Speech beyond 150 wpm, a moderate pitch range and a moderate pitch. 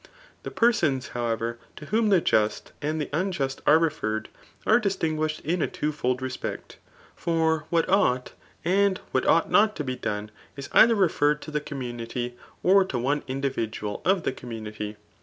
No: average, 170 wpm; wide, 5.9 semitones; medium, 150 Hz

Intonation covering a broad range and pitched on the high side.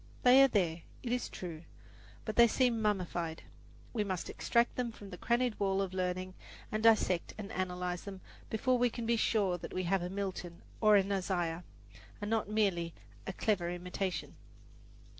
No: average, 3.6 semitones; high, 195 Hz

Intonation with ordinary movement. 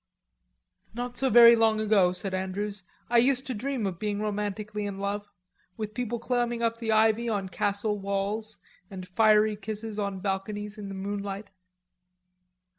No: narrow, 2.1 semitones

